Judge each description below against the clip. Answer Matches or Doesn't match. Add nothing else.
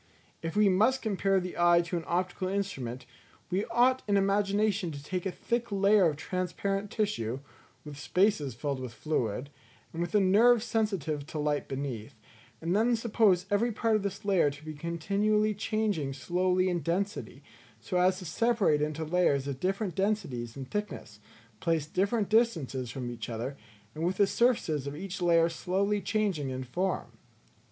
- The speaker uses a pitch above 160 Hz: Matches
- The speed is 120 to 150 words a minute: Doesn't match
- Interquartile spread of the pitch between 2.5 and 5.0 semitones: Doesn't match